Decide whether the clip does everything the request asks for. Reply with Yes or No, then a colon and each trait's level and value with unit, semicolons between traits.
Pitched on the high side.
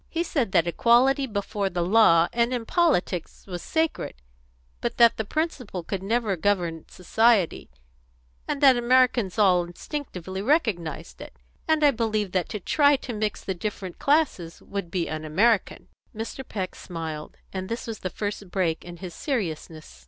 Yes: high, 205 Hz